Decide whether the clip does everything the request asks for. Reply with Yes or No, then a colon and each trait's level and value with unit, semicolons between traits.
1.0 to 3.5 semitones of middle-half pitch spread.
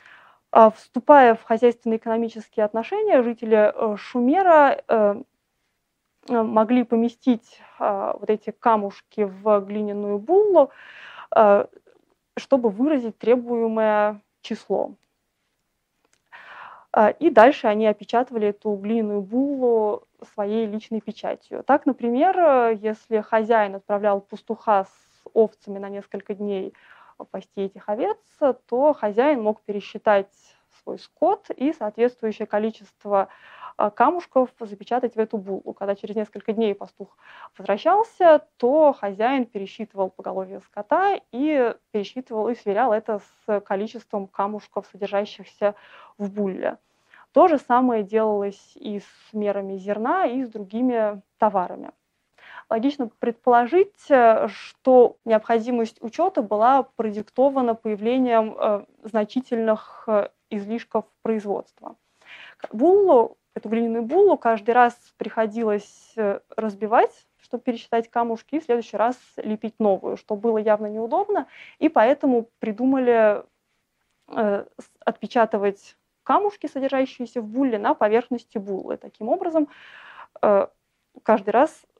Yes: average, 3.2 semitones